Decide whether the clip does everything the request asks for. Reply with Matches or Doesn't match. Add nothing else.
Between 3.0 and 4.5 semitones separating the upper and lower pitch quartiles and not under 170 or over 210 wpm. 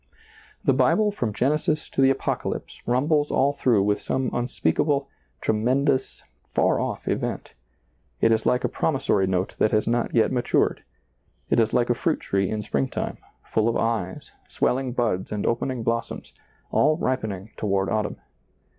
Doesn't match